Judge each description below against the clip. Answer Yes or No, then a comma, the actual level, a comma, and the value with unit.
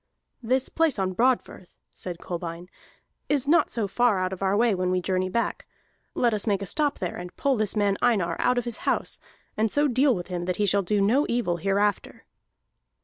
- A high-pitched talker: Yes, high, 205 Hz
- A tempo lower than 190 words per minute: No, fast, 205 wpm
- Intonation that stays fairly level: No, average, 4.8 semitones